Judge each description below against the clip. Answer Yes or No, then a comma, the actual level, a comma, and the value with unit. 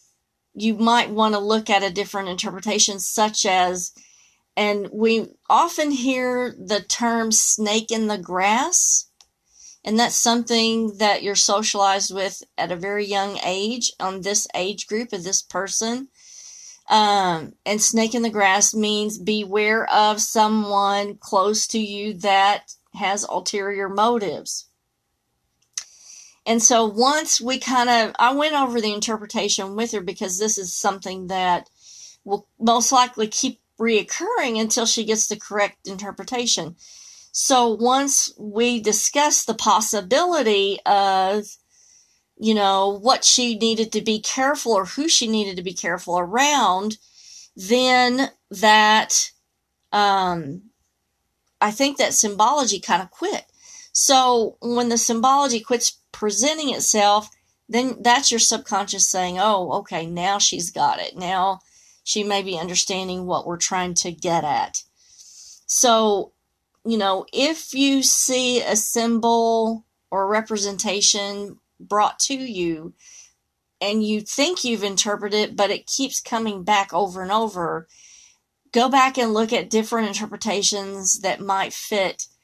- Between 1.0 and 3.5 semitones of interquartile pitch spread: Yes, average, 3.1 semitones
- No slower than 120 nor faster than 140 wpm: Yes, slow, 135 wpm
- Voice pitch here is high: Yes, high, 215 Hz